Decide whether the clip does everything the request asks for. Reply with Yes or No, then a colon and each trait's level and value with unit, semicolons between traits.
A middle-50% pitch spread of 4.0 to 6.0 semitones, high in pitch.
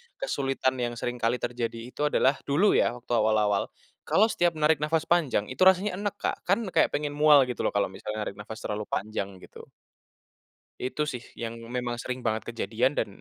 No: average, 4.9 semitones; low, 125 Hz